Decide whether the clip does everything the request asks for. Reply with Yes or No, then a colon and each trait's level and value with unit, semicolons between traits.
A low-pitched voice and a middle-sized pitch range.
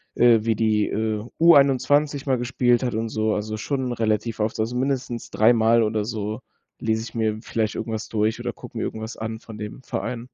No: low, 115 Hz; narrow, 2.2 semitones